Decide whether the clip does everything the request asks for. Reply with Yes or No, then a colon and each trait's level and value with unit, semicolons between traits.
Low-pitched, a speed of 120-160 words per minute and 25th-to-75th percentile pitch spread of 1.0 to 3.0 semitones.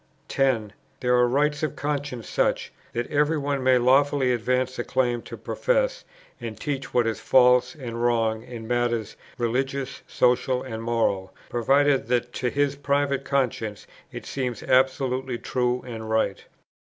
Yes: low, 125 Hz; average, 150 wpm; narrow, 2.6 semitones